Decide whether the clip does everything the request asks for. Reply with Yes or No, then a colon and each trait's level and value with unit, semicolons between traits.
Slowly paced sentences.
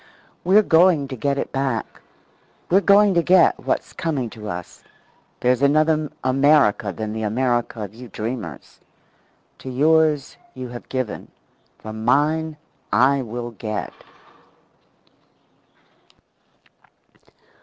Yes: slow, 110 wpm